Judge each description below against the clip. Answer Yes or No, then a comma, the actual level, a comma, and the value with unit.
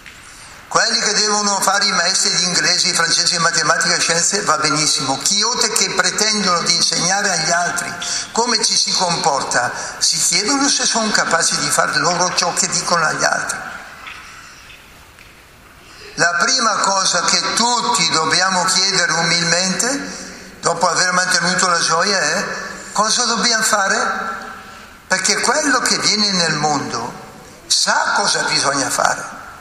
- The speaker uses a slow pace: No, average, 135 wpm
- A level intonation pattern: No, average, 3.7 semitones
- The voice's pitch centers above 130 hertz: Yes, high, 190 Hz